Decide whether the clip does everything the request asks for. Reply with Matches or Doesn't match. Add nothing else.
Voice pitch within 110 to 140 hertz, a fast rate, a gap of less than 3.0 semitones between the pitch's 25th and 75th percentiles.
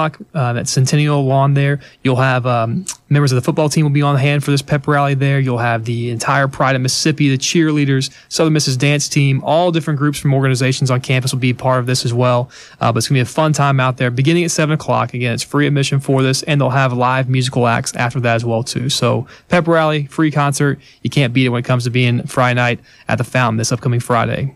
Matches